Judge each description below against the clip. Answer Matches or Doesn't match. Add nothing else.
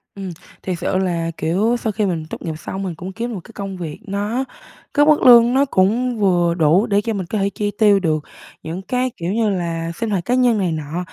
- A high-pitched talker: Matches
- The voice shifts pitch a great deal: Doesn't match